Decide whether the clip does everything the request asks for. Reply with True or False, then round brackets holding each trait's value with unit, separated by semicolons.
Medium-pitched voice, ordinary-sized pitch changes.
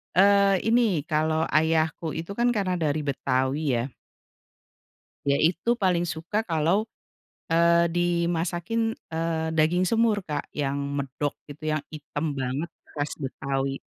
True (160 Hz; 3.5 semitones)